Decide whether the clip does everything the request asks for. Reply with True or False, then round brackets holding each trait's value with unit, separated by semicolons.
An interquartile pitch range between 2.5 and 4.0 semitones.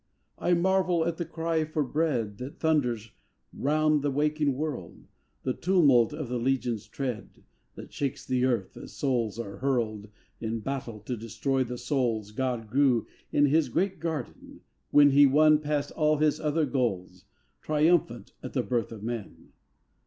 False (4.6 semitones)